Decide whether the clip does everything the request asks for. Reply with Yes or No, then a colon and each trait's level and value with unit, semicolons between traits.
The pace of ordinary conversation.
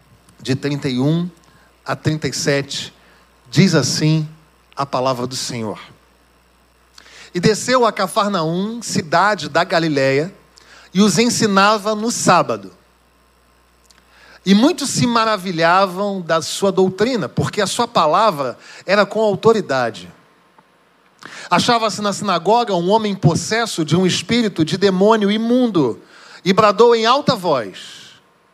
No: slow, 110 wpm